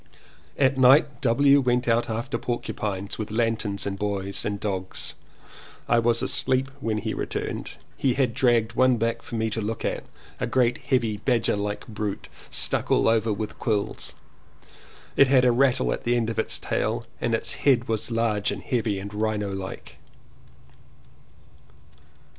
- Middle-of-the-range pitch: No, low, 115 Hz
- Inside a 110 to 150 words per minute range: No, average, 165 wpm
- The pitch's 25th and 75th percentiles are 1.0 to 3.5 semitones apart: Yes, average, 3.0 semitones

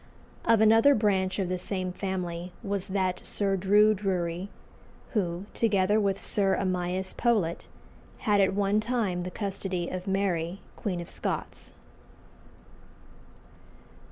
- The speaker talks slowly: Yes, slow, 125 wpm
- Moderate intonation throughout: No, narrow, 2.1 semitones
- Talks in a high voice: Yes, high, 195 Hz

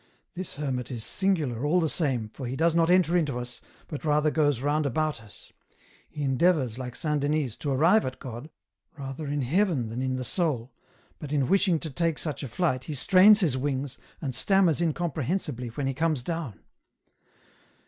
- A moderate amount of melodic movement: Yes, average, 4.3 semitones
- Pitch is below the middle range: No, medium, 145 Hz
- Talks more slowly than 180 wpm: No, average, 185 wpm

